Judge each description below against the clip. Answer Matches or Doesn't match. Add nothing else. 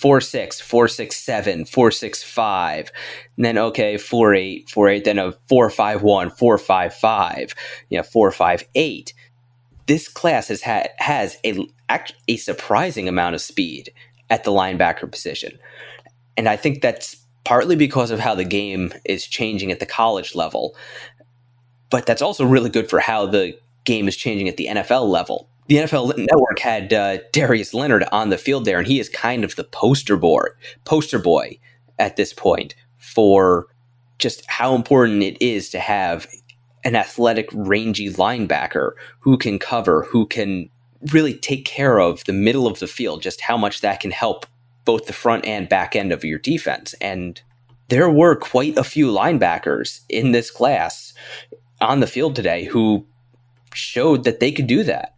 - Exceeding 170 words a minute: Doesn't match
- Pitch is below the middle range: Matches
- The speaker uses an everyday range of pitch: Matches